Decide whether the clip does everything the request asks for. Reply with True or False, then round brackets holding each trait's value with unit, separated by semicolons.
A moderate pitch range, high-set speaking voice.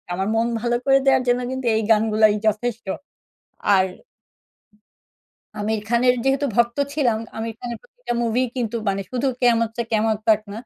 False (2.3 semitones; 235 Hz)